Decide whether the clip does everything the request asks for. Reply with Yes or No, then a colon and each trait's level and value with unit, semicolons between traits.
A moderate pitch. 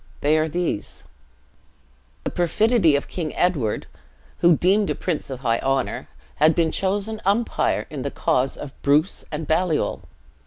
Yes: medium, 160 Hz